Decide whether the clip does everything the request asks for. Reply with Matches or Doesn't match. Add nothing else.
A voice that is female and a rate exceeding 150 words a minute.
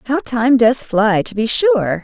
Matches